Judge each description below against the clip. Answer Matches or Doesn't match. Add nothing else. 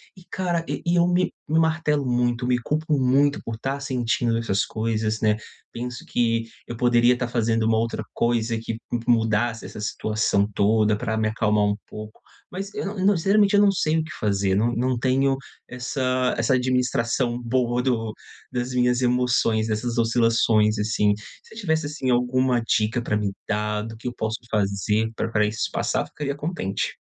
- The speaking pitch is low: Matches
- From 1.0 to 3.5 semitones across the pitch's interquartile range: Matches